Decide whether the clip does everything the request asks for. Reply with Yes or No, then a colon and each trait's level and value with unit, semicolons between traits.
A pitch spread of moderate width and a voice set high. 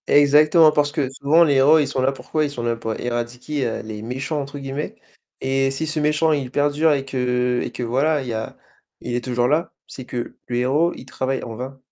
No: average, 3.2 semitones; low, 135 Hz